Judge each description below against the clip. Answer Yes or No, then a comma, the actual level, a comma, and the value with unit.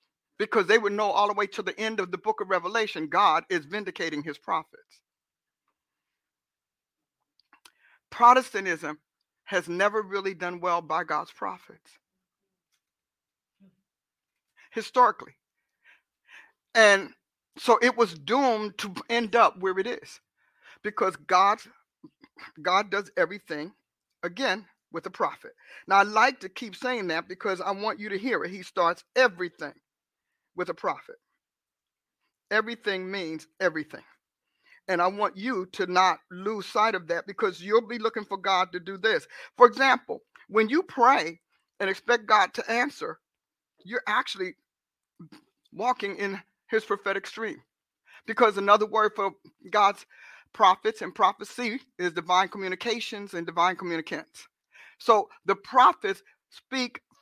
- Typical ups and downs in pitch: Yes, average, 4.3 semitones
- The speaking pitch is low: No, high, 200 Hz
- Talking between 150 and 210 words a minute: No, slow, 135 wpm